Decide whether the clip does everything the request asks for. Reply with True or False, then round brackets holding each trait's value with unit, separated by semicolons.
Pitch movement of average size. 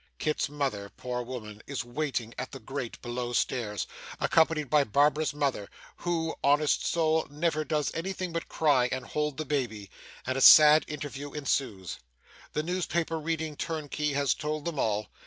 True (3.7 semitones)